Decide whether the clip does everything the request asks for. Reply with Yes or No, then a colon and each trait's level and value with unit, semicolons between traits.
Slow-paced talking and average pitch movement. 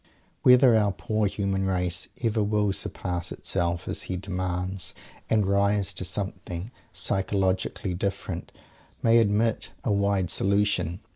No: slow, 125 wpm; narrow, 2.2 semitones